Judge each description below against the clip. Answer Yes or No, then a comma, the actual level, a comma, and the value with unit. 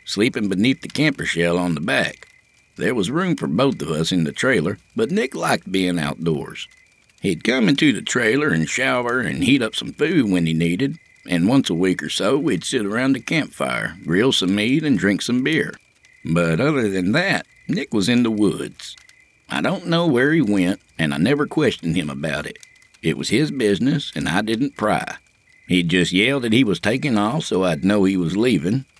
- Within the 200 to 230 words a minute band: Yes, fast, 205 wpm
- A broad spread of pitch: Yes, wide, 6.4 semitones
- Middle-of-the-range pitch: No, very low, 95 Hz